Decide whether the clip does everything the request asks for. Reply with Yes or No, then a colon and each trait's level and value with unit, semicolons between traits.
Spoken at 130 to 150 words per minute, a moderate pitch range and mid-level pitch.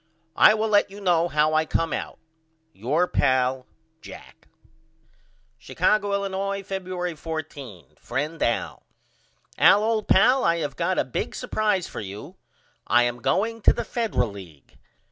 No: average, 145 wpm; wide, 7.6 semitones; medium, 170 Hz